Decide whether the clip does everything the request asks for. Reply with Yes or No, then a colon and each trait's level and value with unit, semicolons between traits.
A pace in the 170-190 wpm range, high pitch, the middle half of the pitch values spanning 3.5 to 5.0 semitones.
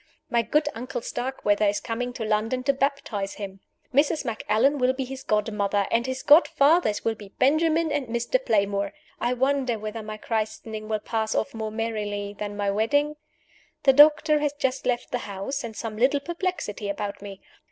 Yes: average, 175 wpm; high, 230 Hz; average, 4.6 semitones